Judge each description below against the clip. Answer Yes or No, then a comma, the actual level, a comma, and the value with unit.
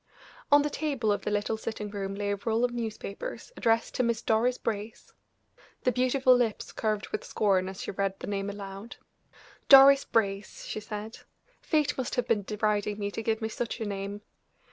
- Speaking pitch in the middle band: No, high, 220 Hz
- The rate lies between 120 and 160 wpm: No, average, 190 wpm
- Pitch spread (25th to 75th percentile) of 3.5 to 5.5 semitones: No, average, 3.0 semitones